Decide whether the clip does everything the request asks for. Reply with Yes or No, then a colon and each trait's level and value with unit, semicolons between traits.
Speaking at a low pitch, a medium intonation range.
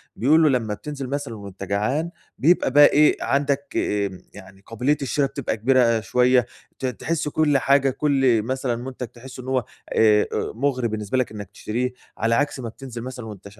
Yes: low, 125 Hz; average, 3.8 semitones